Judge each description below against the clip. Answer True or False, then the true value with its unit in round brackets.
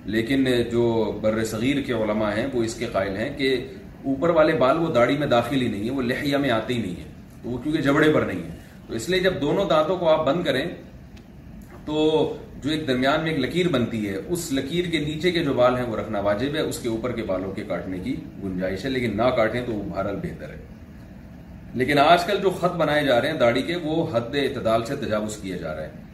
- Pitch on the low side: True (130 Hz)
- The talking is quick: True (240 wpm)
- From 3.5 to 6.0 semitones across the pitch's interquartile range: True (5.6 semitones)